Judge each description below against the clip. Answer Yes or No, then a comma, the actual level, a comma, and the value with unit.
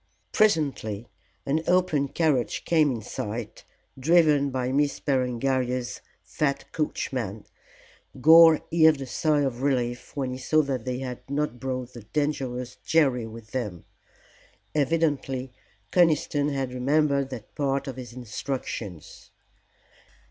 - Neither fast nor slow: No, slow, 120 wpm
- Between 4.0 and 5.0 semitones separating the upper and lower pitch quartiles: No, average, 3.1 semitones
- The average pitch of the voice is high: No, low, 135 Hz